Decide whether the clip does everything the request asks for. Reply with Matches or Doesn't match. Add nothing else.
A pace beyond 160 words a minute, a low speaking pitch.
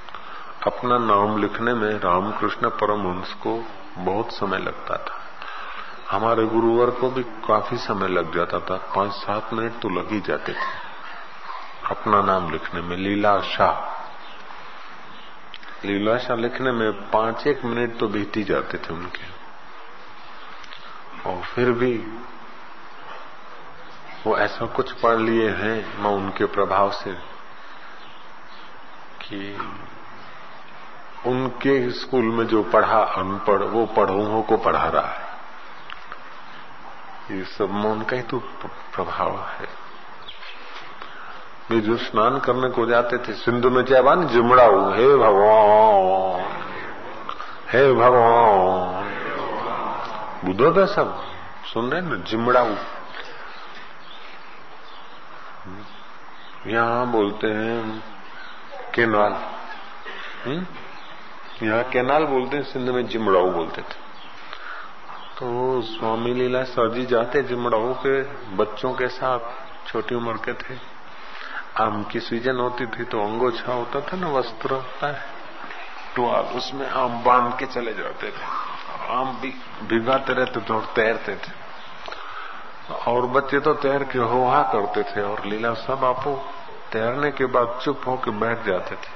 Doesn't match